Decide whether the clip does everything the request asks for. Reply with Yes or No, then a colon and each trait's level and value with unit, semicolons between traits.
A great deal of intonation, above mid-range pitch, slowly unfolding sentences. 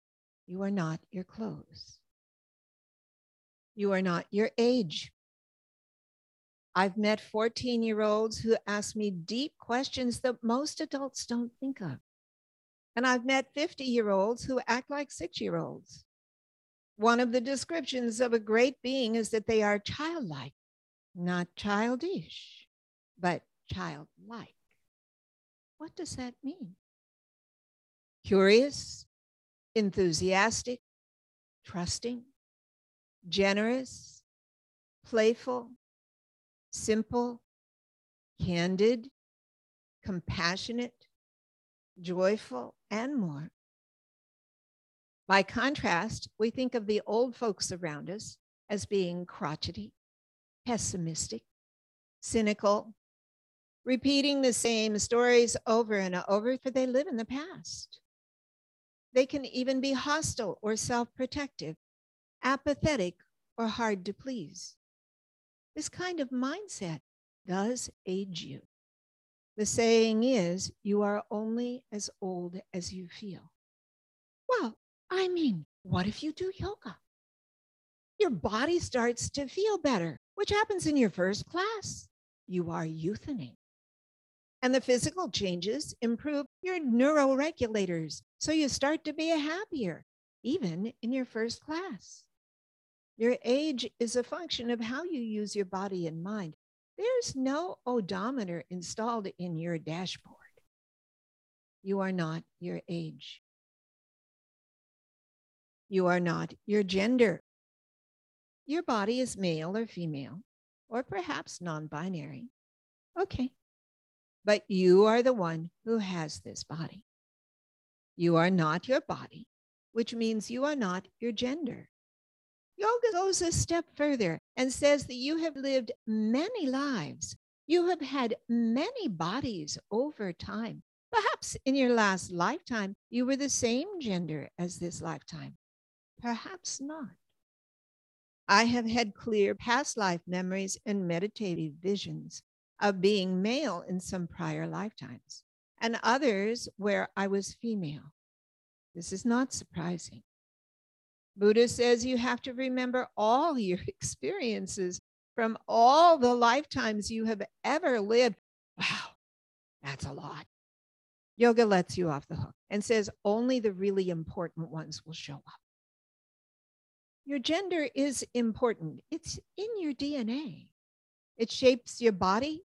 Yes: wide, 5.9 semitones; high, 225 Hz; slow, 120 wpm